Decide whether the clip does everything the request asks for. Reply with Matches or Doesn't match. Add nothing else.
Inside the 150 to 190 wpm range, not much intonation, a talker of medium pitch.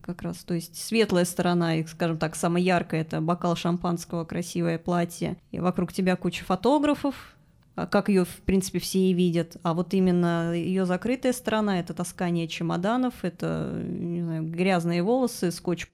Matches